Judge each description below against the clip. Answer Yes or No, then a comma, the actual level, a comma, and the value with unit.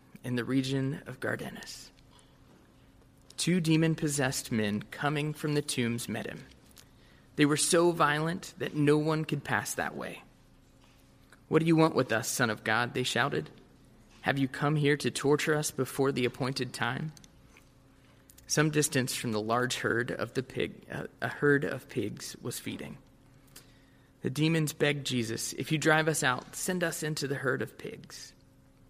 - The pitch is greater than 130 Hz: Yes, medium, 140 Hz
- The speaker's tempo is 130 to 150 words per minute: No, average, 160 wpm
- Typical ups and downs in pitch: Yes, average, 3.5 semitones